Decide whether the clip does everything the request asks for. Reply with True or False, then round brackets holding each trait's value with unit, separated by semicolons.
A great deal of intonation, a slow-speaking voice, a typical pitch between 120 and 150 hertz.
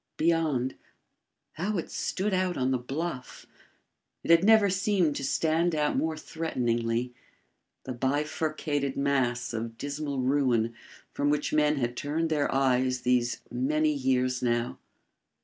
False (4.1 semitones; 130 wpm; 140 Hz)